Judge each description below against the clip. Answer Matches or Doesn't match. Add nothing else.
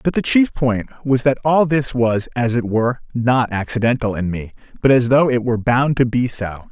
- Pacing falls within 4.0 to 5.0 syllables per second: Matches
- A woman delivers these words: Doesn't match